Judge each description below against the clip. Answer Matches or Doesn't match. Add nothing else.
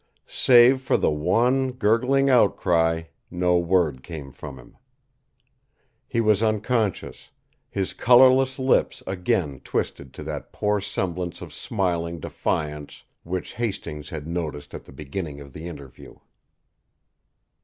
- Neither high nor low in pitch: Doesn't match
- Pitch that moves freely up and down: Matches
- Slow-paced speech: Matches